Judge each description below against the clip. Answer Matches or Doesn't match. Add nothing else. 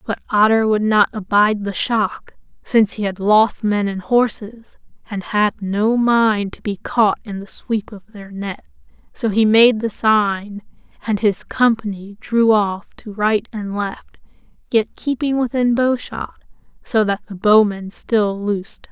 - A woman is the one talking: Matches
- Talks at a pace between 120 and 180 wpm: Matches